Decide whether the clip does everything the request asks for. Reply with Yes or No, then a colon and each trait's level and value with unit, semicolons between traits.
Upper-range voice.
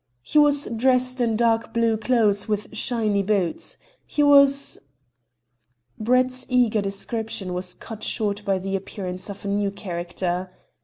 Yes: high, 210 Hz